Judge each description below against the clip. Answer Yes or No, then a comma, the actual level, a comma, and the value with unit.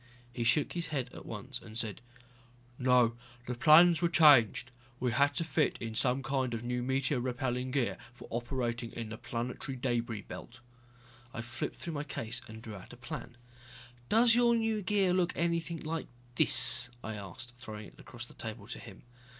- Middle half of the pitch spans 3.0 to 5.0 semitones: Yes, average, 4.6 semitones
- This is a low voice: Yes, low, 125 Hz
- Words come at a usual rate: Yes, average, 185 wpm